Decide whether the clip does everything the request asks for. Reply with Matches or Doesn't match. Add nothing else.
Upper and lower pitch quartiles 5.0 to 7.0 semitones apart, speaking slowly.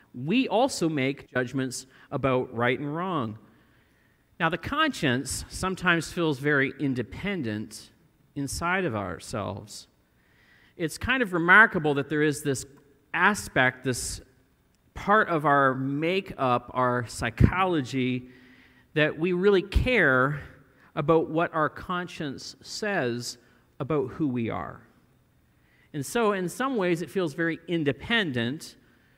Matches